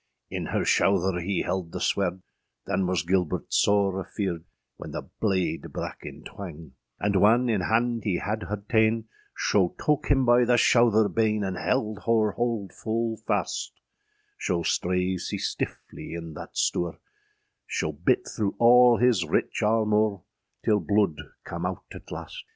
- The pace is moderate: Yes, average, 155 wpm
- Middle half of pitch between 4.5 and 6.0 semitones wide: No, average, 3.7 semitones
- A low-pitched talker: Yes, low, 100 Hz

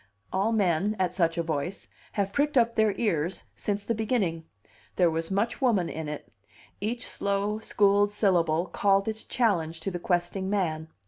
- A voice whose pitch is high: Yes, high, 195 Hz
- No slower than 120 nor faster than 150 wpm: No, average, 165 wpm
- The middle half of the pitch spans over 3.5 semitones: Yes, average, 3.9 semitones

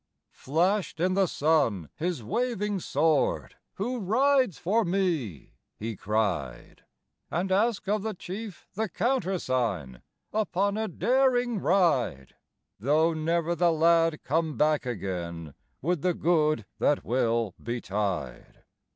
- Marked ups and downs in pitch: Yes, wide, 8.8 semitones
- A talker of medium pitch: Yes, medium, 165 Hz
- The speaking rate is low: Yes, slow, 115 wpm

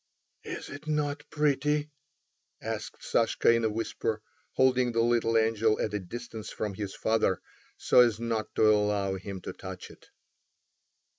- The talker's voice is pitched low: Yes, low, 115 Hz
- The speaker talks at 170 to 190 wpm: No, average, 150 wpm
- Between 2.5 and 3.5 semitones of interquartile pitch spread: Yes, average, 3.1 semitones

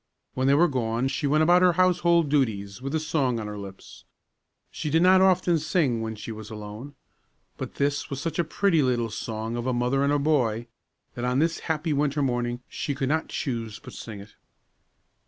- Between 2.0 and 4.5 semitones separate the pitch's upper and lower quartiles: No, average, 5.3 semitones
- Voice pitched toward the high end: No, low, 135 Hz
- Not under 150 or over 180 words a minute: No, fast, 205 wpm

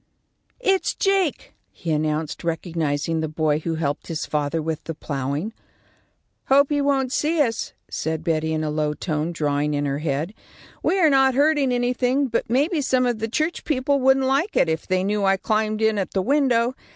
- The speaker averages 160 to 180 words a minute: No, average, 190 wpm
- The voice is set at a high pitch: Yes, high, 205 Hz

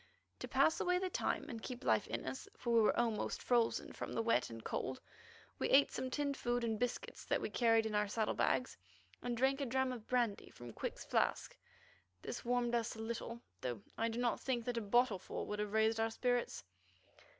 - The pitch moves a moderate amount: No, narrow, 2.2 semitones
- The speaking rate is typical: No, fast, 210 wpm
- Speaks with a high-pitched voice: Yes, high, 235 Hz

